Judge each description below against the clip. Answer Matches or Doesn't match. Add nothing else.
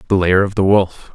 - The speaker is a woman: Doesn't match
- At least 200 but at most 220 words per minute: Doesn't match